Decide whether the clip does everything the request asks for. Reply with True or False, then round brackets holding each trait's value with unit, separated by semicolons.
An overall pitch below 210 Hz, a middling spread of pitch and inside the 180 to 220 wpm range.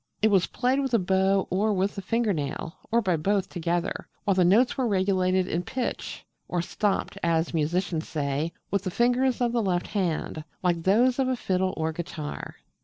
True (190 Hz; 4.2 semitones; 190 wpm)